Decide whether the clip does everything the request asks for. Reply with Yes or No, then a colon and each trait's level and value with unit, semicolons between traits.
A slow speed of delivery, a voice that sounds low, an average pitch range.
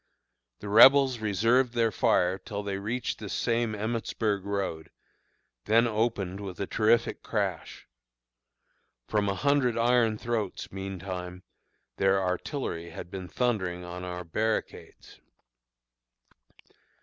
Yes: slow, 115 wpm; low, 105 Hz; average, 3.7 semitones